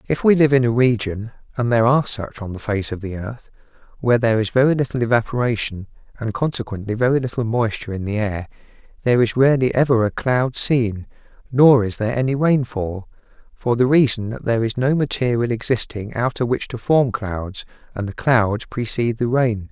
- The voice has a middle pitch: No, low, 120 Hz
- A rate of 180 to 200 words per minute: Yes, average, 185 wpm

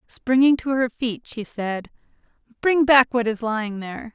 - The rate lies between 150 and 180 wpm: Yes, average, 175 wpm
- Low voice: No, high, 240 Hz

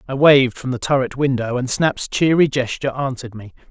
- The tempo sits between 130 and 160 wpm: No, average, 195 wpm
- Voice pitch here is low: Yes, low, 130 Hz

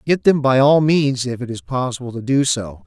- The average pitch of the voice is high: No, low, 125 Hz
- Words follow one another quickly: Yes, fast, 250 wpm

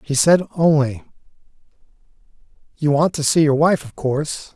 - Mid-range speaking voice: Yes, medium, 150 Hz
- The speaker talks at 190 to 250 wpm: No, average, 145 wpm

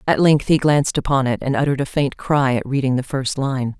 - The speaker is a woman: Yes, female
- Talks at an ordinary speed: No, fast, 255 wpm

